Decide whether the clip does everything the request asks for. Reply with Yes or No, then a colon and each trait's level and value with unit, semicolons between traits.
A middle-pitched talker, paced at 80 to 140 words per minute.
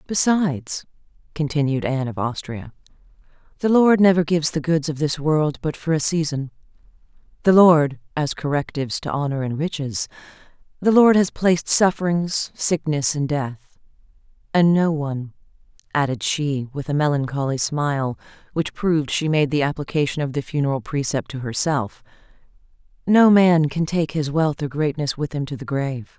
No: medium, 150 Hz; average, 150 wpm